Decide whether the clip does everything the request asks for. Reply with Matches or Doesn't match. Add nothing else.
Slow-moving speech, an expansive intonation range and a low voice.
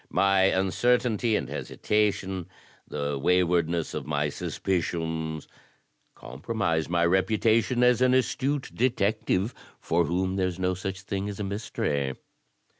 Doesn't match